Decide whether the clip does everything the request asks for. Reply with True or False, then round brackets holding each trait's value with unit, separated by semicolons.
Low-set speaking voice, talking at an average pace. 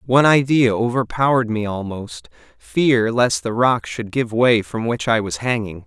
True (115 Hz; 175 wpm)